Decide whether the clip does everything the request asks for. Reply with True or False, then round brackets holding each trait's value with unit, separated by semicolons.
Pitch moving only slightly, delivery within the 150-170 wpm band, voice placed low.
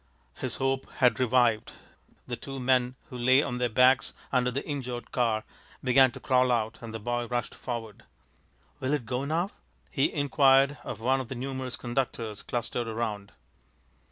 True (2.1 semitones; 165 wpm; 125 Hz)